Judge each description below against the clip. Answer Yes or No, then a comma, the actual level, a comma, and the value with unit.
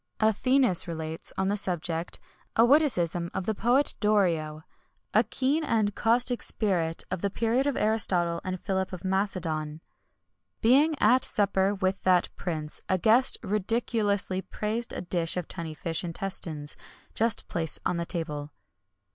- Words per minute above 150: No, average, 145 wpm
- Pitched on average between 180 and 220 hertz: Yes, high, 190 Hz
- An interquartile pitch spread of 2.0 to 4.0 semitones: No, average, 4.8 semitones